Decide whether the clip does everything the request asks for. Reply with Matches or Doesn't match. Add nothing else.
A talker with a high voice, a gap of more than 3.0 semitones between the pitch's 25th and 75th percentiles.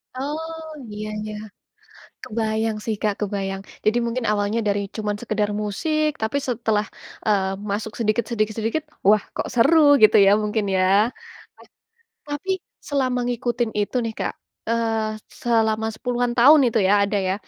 Doesn't match